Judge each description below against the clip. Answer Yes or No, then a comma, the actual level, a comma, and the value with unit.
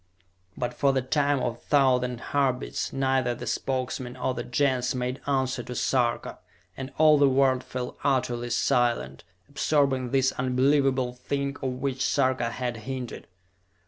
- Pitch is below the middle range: Yes, low, 130 Hz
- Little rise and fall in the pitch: Yes, narrow, 1.6 semitones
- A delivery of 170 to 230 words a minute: No, average, 145 wpm